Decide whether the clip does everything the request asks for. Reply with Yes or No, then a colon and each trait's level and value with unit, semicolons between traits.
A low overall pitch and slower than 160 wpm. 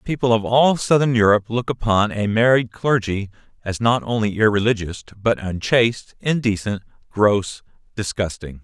Yes: low, 110 Hz; average, 140 wpm